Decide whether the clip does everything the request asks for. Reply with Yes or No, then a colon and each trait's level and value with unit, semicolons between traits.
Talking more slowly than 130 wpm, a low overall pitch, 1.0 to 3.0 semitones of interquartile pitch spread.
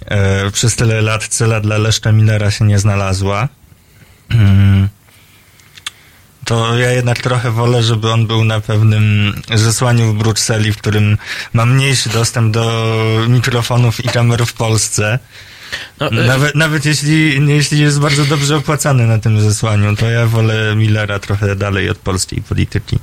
No: average, 140 wpm; low, 110 Hz; narrow, 2.5 semitones